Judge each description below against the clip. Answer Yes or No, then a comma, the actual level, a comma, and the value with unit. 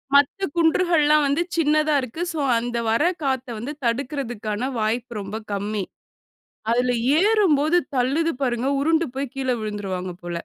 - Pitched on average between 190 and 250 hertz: No, very high, 265 Hz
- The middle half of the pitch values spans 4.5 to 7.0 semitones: Yes, average, 5.2 semitones